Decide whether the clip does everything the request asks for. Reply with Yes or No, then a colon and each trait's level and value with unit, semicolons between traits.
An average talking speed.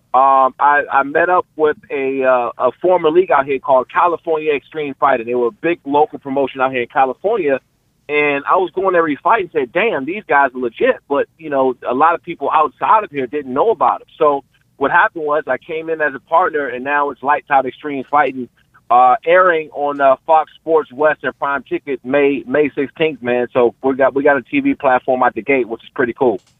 No: fast, 225 wpm